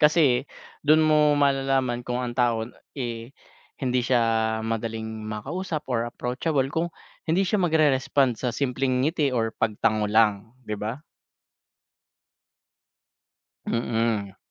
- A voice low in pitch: Yes, low, 125 Hz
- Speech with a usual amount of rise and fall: Yes, average, 4.2 semitones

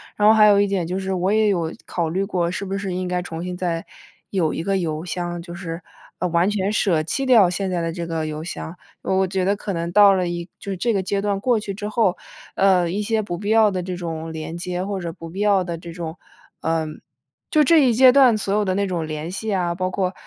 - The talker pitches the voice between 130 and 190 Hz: Yes, medium, 185 Hz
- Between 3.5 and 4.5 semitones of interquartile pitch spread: No, average, 2.9 semitones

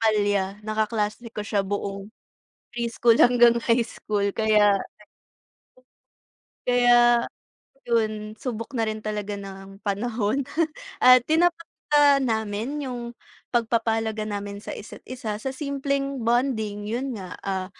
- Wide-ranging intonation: No, average, 3.0 semitones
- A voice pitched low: No, high, 225 Hz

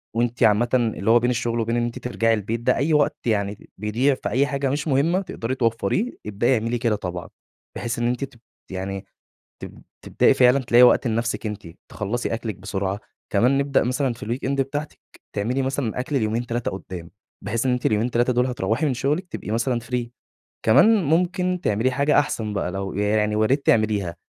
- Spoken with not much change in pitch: No, average, 3.8 semitones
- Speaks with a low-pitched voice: Yes, low, 120 Hz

